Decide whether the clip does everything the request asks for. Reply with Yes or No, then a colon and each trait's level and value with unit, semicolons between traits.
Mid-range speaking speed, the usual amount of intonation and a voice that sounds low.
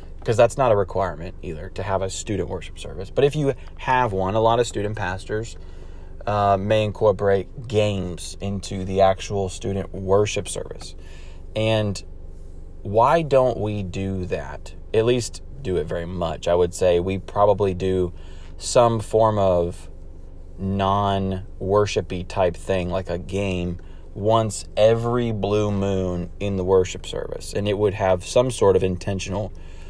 Yes: average, 150 wpm; average, 3.3 semitones; very low, 95 Hz